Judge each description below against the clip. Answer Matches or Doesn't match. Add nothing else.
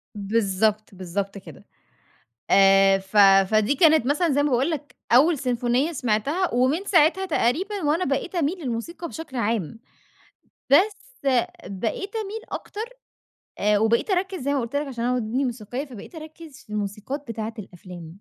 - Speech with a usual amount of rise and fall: Doesn't match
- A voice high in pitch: Matches